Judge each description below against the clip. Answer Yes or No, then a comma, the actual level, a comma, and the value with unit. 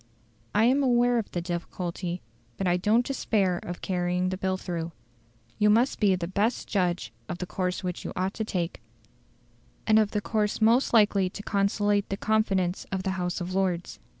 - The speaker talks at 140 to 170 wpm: No, average, 185 wpm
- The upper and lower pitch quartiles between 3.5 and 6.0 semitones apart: No, average, 3.1 semitones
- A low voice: No, high, 190 Hz